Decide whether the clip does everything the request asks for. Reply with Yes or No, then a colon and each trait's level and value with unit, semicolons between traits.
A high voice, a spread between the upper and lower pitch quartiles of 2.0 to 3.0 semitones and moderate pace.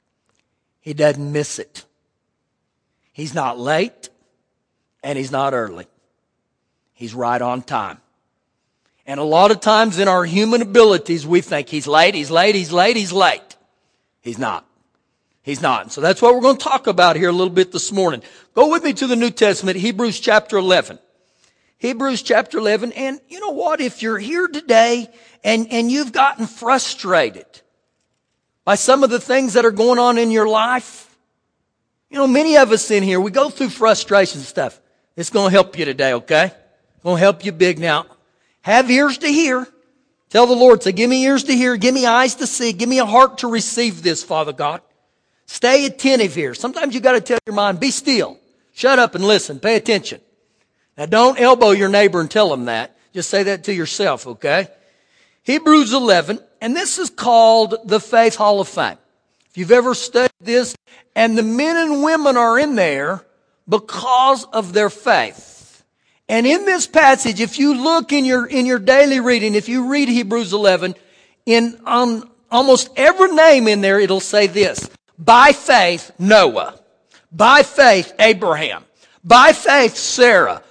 No: high, 225 Hz; average, 5.2 semitones; average, 180 wpm